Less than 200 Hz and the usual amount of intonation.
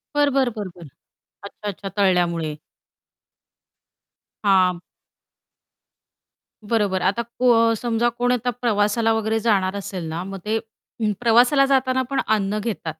No: high, 215 Hz; average, 3.7 semitones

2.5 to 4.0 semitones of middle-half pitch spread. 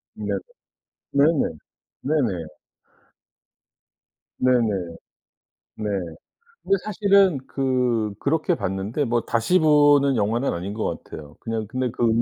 No: wide, 5.6 semitones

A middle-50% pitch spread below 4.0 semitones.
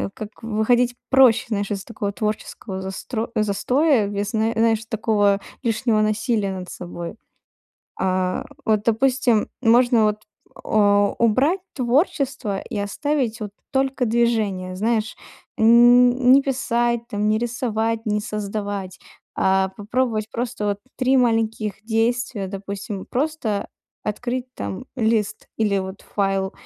Yes: average, 3.0 semitones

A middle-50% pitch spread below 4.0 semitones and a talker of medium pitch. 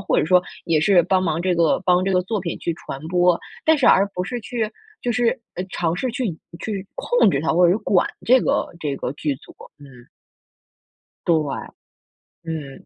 No: average, 4.4 semitones; medium, 180 Hz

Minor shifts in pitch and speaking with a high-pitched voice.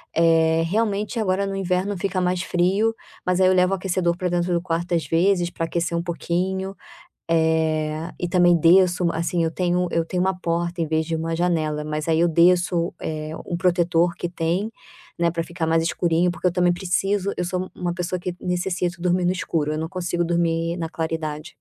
No: narrow, 1.7 semitones; medium, 175 Hz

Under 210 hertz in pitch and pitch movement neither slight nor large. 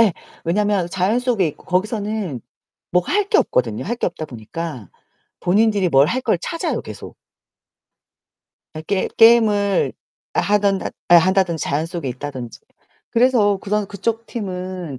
Yes: high, 190 Hz; average, 4.5 semitones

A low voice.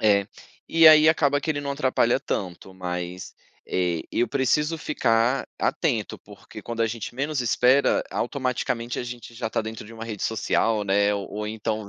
Yes: low, 115 Hz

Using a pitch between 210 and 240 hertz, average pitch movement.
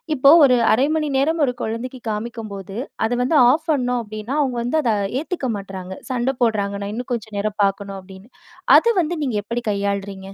Yes: high, 230 Hz; average, 4.3 semitones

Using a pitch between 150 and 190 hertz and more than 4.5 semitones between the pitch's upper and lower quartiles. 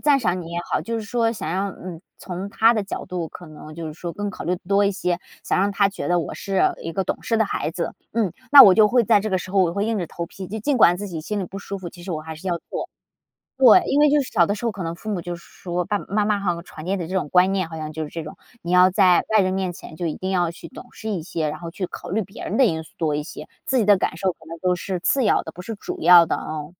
No: medium, 185 Hz; average, 3.3 semitones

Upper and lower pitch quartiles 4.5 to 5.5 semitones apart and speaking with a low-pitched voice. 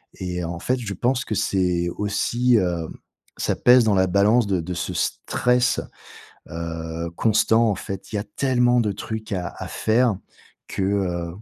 Yes: average, 4.9 semitones; low, 100 Hz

